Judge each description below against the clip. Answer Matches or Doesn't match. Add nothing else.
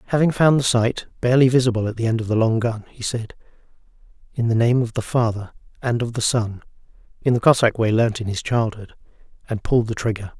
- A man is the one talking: Matches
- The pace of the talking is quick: Matches